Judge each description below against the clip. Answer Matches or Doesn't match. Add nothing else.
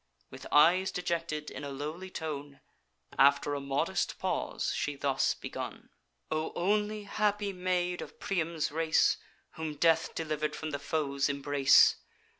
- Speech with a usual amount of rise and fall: Matches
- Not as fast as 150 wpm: Matches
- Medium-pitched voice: Matches